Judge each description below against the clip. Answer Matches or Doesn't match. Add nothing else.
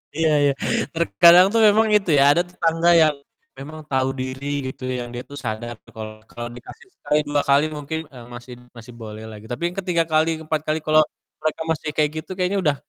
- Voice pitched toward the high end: Doesn't match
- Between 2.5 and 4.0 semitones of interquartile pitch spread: Doesn't match